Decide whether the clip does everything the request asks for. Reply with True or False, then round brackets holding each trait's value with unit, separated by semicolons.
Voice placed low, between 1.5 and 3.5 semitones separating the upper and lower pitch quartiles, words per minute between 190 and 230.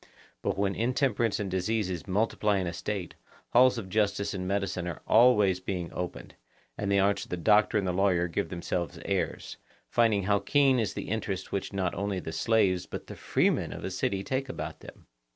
True (100 Hz; 2.8 semitones; 195 wpm)